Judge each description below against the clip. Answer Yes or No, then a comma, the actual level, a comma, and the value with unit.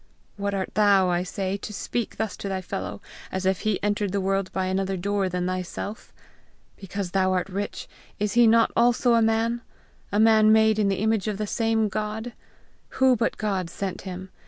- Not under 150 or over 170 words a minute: No, average, 195 wpm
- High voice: Yes, high, 200 Hz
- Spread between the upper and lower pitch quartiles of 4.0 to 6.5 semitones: No, narrow, 2.5 semitones